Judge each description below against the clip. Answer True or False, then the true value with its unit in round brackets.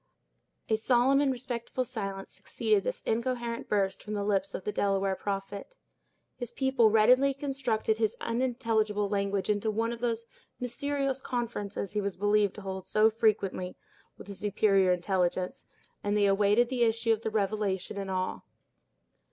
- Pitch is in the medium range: False (215 Hz)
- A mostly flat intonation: False (3.2 semitones)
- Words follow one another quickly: False (155 wpm)